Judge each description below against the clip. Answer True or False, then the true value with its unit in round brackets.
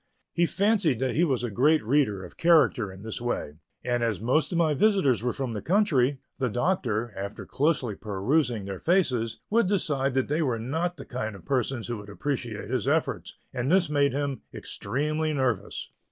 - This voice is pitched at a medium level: False (130 Hz)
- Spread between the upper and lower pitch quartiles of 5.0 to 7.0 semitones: True (5.6 semitones)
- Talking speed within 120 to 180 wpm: False (190 wpm)